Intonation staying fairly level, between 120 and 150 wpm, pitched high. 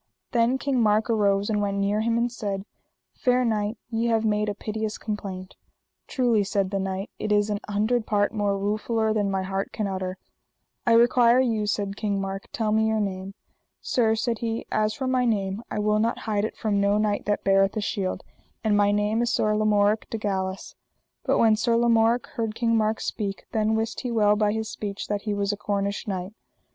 No: narrow, 1.8 semitones; fast, 205 wpm; high, 210 Hz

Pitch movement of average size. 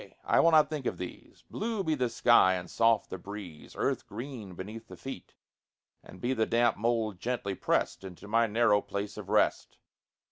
Yes: average, 3.7 semitones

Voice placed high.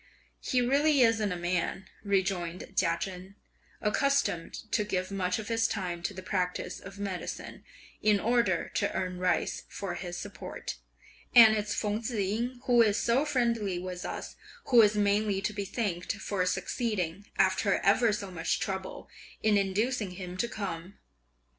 Yes: high, 200 Hz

